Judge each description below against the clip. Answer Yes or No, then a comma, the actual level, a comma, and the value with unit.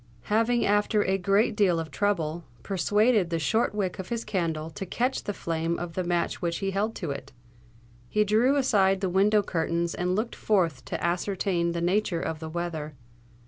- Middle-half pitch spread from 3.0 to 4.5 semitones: Yes, average, 3.6 semitones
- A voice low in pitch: No, medium, 185 Hz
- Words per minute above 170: Yes, average, 185 wpm